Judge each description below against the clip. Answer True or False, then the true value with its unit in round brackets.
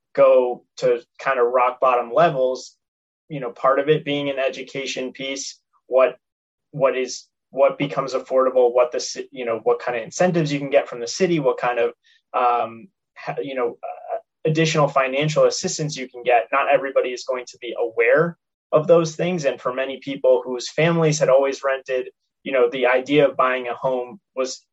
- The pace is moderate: True (185 wpm)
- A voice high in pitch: False (135 Hz)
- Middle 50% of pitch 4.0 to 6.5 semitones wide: True (4.6 semitones)